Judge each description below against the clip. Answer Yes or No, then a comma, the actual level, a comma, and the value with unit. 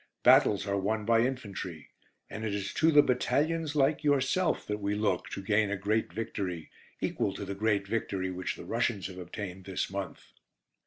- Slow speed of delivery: No, average, 180 wpm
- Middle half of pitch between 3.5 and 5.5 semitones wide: Yes, average, 3.9 semitones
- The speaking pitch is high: No, low, 105 Hz